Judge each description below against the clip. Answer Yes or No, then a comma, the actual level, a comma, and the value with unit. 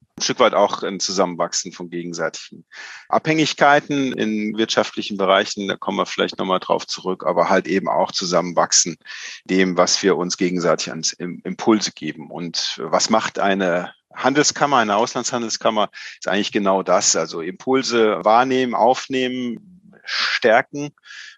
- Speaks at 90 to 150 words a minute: Yes, average, 135 wpm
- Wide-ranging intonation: Yes, wide, 6.1 semitones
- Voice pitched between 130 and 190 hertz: No, low, 110 Hz